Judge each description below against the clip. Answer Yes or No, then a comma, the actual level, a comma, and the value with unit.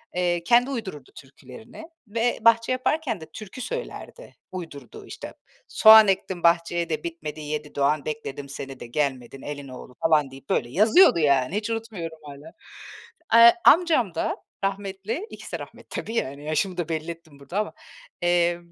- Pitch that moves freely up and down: Yes, wide, 7.0 semitones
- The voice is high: No, medium, 170 Hz